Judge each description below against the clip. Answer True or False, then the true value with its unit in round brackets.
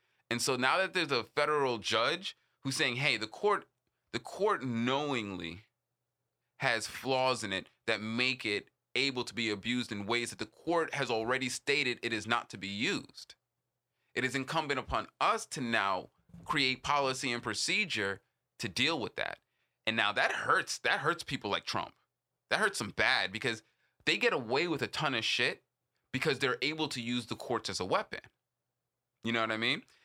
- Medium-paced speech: True (185 wpm)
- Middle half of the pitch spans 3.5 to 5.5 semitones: False (3.0 semitones)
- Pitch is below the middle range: True (125 Hz)